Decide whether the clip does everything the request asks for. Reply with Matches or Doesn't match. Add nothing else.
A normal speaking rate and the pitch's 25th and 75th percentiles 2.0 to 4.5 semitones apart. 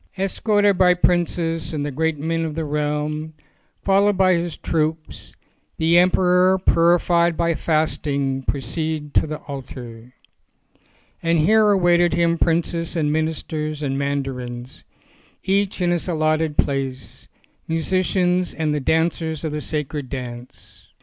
Doesn't match